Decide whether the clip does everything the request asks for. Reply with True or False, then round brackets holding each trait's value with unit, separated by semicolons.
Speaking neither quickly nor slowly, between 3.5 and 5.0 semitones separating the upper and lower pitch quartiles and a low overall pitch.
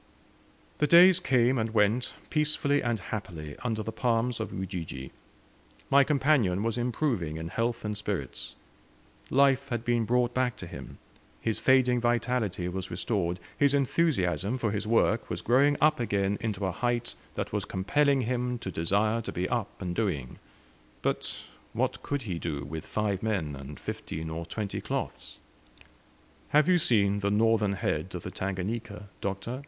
True (160 wpm; 4.7 semitones; 110 Hz)